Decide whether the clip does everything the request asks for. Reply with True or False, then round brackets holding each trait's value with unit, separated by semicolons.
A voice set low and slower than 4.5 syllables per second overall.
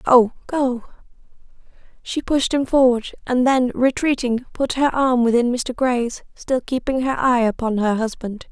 False (250 Hz; 4.3 syllables/s)